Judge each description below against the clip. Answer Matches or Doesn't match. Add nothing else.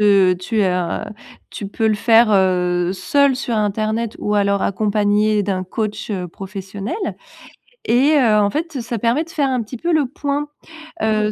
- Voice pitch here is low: Doesn't match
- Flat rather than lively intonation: Doesn't match